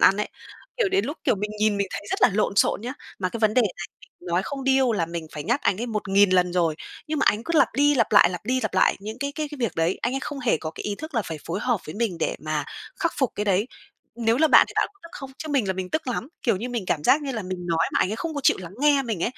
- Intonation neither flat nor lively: No, wide, 6.4 semitones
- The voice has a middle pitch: No, high, 220 Hz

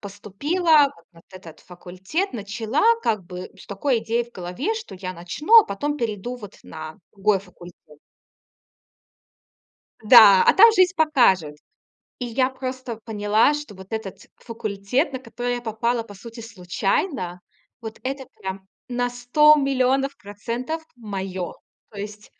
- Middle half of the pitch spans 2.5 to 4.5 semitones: No, average, 5.2 semitones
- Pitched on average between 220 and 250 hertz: Yes, high, 225 Hz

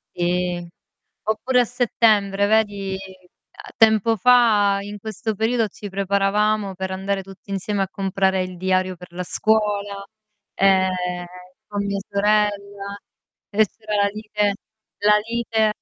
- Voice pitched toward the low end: No, high, 200 Hz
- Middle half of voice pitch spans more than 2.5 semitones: No, narrow, 2.1 semitones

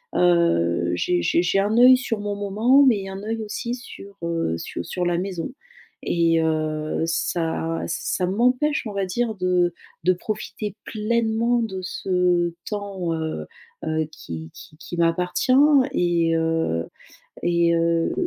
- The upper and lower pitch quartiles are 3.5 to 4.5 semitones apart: Yes, average, 4.2 semitones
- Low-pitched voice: No, medium, 180 Hz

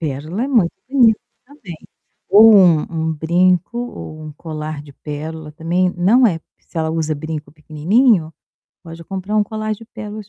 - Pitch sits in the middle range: Yes, medium, 170 Hz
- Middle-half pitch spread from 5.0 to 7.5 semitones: Yes, average, 5.3 semitones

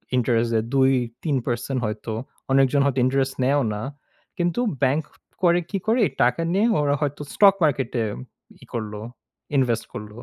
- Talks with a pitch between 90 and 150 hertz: Yes, low, 135 Hz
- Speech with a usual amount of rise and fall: Yes, average, 3.5 semitones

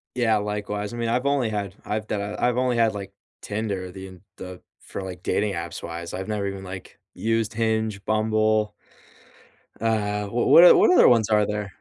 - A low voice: Yes, low, 105 Hz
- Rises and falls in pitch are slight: Yes, narrow, 2.1 semitones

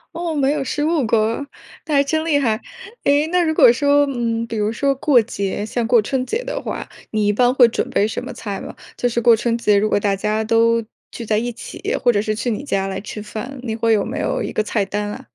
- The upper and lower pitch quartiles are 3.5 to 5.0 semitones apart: Yes, average, 4.5 semitones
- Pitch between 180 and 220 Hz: No, high, 230 Hz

